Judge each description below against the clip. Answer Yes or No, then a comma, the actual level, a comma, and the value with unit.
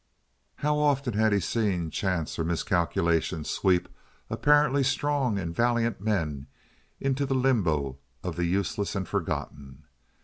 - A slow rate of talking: Yes, slow, 130 wpm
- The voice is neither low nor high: No, low, 100 Hz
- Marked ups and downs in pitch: Yes, wide, 7.6 semitones